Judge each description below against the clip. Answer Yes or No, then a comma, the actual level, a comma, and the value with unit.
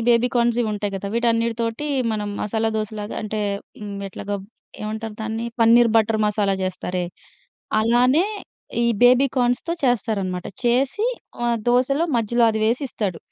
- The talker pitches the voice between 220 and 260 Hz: Yes, high, 225 Hz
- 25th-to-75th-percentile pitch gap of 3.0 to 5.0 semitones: No, narrow, 2.4 semitones